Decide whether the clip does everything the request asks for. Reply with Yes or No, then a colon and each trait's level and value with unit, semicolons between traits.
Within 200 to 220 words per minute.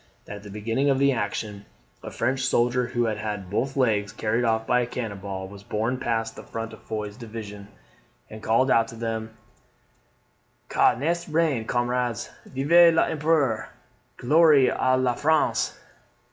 No: average, 165 wpm